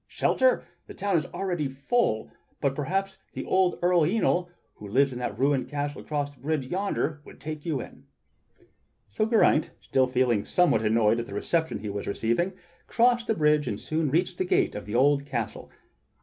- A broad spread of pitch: Yes, wide, 5.9 semitones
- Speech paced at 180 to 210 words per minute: Yes, average, 185 wpm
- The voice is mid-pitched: Yes, medium, 145 Hz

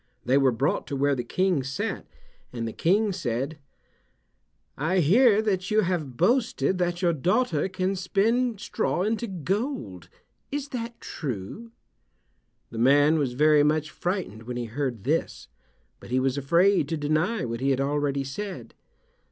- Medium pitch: Yes, medium, 155 Hz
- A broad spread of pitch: Yes, wide, 6.4 semitones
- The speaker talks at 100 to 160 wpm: Yes, average, 155 wpm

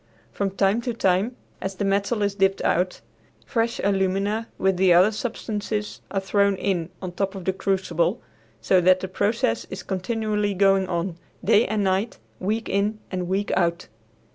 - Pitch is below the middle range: No, high, 195 Hz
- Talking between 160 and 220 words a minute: Yes, average, 165 wpm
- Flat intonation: Yes, narrow, 1.9 semitones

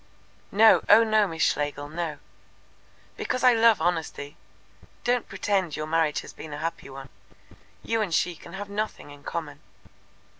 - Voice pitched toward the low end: No, medium, 170 Hz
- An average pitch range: No, wide, 6.0 semitones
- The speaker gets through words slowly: No, average, 155 wpm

